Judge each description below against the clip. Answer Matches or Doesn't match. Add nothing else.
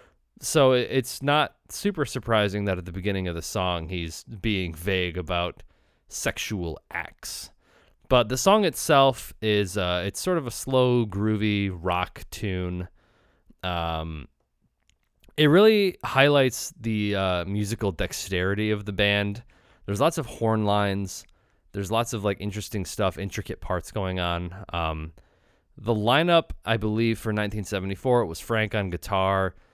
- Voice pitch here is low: Matches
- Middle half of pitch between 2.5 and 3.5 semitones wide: Doesn't match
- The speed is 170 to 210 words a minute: Doesn't match